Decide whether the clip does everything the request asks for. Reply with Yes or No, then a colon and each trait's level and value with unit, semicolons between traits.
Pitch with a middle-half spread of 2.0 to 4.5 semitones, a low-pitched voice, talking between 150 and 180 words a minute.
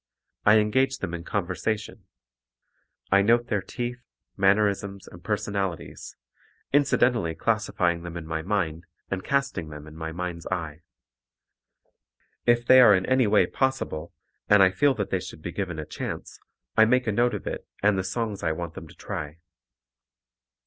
No: average, 5.1 semitones; low, 100 Hz; average, 165 wpm